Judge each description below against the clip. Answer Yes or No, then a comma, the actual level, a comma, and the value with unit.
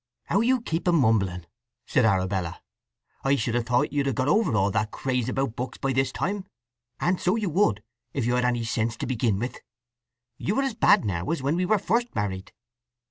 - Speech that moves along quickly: Yes, fast, 210 wpm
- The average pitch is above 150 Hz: No, low, 130 Hz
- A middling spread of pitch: No, wide, 8.1 semitones